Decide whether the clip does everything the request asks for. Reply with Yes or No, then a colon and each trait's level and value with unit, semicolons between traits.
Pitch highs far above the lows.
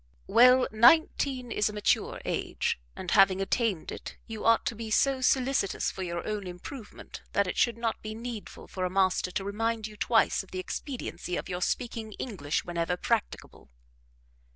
No: average, 4.0 semitones